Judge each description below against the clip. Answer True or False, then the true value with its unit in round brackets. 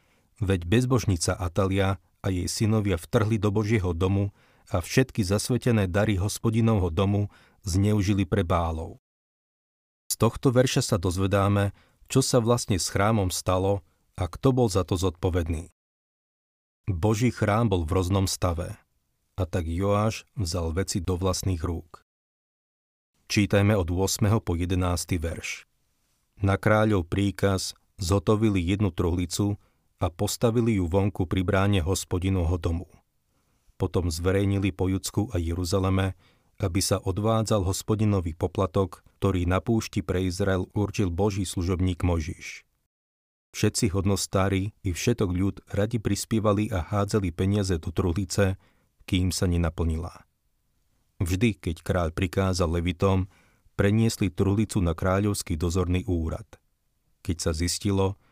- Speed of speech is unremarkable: True (120 wpm)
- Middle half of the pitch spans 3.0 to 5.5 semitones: False (2.4 semitones)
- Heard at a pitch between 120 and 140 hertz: False (95 Hz)